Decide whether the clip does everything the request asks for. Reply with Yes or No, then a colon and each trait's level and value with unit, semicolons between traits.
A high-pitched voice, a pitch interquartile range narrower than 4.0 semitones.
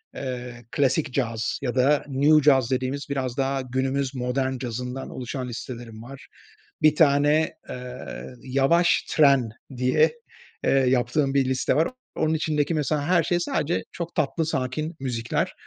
No: low, 135 Hz; average, 2.8 semitones